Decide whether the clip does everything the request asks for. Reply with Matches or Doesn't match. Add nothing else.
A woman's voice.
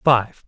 Doesn't match